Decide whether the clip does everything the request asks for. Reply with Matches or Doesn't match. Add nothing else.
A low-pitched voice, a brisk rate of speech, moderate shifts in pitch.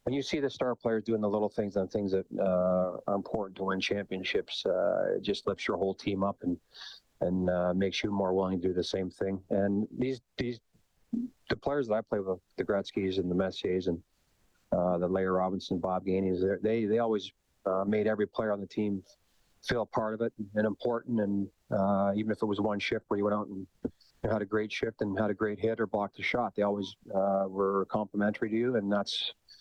Doesn't match